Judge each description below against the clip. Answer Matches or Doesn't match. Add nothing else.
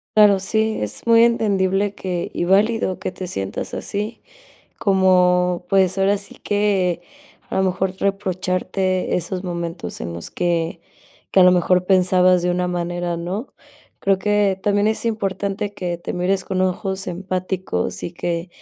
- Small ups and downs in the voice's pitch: Matches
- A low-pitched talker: Doesn't match